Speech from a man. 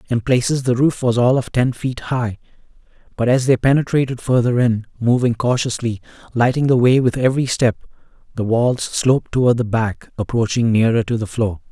Yes: male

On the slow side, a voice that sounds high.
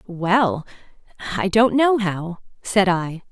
Yes: slow, 110 wpm; high, 195 Hz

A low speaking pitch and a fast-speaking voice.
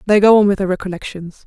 No: high, 195 Hz; fast, 245 wpm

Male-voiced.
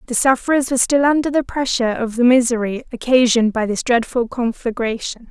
No: female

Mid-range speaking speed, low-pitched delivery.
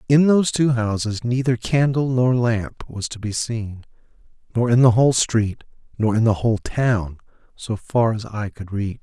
Yes: average, 185 wpm; low, 115 Hz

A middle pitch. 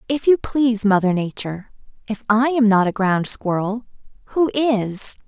No: high, 225 Hz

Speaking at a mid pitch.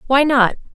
No: very high, 260 Hz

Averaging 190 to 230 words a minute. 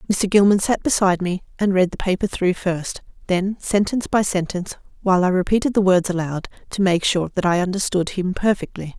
Yes: average, 195 wpm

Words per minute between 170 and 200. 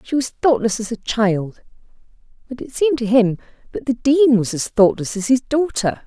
Yes: average, 190 wpm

